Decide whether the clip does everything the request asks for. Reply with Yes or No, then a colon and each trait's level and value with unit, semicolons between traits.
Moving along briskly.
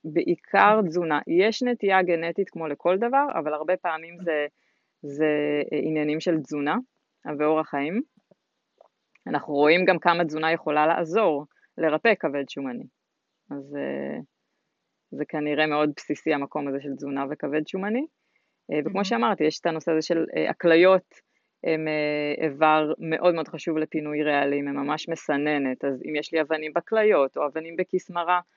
No: average, 140 wpm